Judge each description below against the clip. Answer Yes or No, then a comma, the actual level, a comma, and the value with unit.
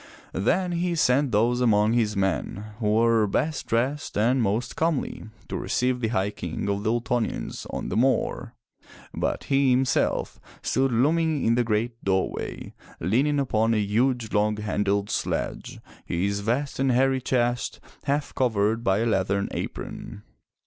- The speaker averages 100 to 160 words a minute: Yes, average, 150 wpm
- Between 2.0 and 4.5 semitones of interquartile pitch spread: Yes, average, 3.9 semitones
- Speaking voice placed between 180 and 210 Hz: No, low, 115 Hz